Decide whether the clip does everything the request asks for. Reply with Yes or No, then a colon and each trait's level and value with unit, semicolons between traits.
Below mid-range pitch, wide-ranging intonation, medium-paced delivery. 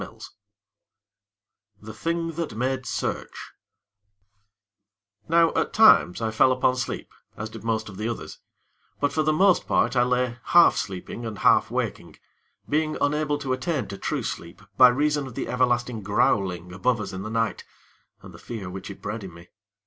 Yes: low, 120 Hz; wide, 5.7 semitones; average, 170 wpm